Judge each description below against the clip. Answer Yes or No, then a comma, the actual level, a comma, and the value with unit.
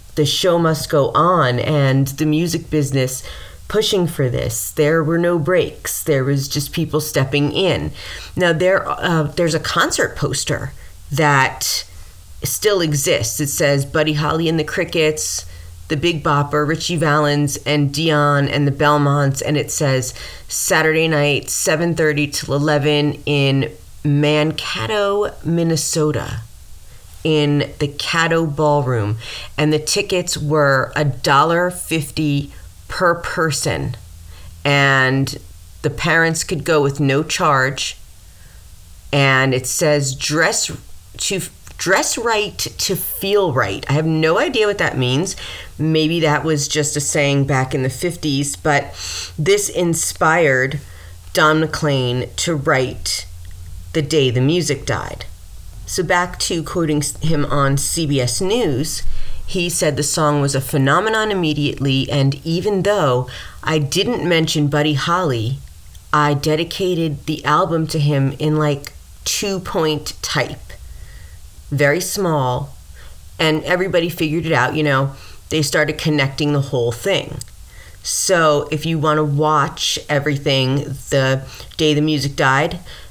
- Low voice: No, medium, 145 Hz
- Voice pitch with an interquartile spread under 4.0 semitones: Yes, average, 3.5 semitones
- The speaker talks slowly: Yes, slow, 130 wpm